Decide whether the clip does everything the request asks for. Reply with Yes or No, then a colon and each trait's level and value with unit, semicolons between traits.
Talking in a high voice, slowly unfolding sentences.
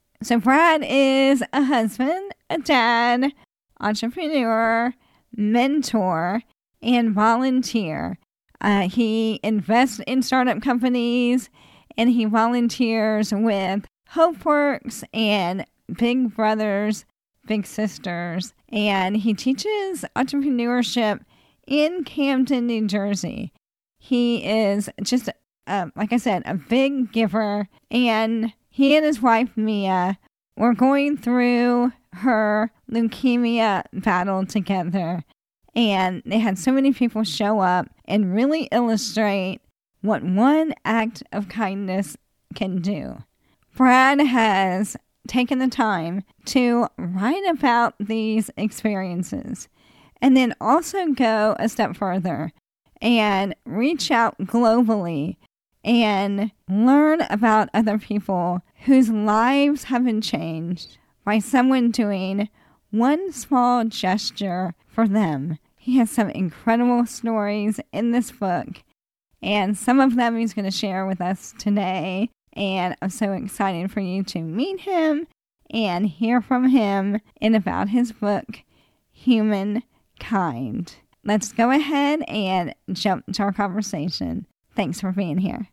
Yes: high, 225 Hz; slow, 115 wpm